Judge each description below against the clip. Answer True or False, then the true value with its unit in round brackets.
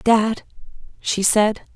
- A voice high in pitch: True (215 Hz)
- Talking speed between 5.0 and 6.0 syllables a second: False (2.9 syllables/s)